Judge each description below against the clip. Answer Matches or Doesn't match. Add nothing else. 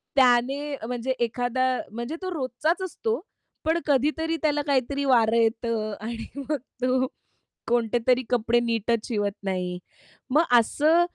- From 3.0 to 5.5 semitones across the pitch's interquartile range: Matches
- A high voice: Matches